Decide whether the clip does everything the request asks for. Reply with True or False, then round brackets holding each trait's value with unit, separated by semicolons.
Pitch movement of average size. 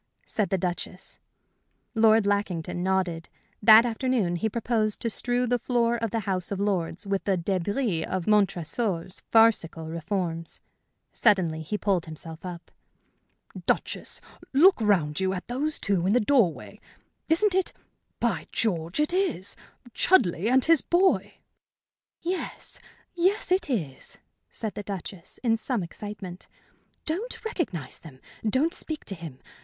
False (5.7 semitones)